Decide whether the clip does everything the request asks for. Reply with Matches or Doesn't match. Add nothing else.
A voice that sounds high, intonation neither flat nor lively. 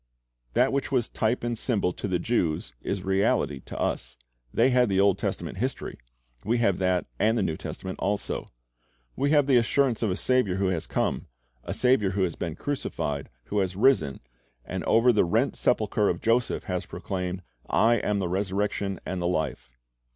Doesn't match